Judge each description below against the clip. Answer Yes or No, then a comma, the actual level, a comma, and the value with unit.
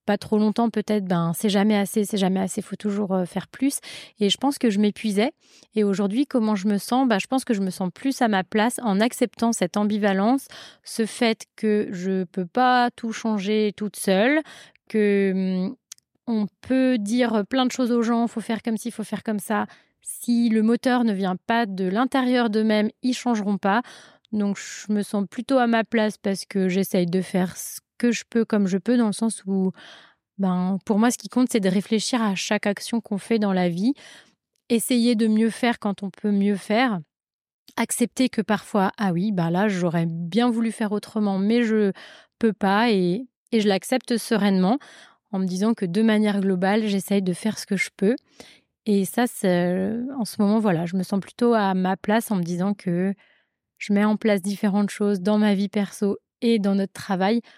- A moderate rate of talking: Yes, average, 210 wpm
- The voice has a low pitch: No, high, 210 Hz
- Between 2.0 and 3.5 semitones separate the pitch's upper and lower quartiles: Yes, average, 3.0 semitones